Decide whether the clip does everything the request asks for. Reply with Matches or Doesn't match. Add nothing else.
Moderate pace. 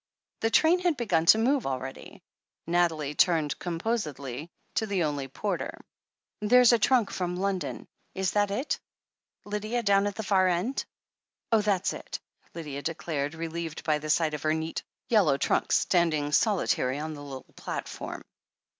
Matches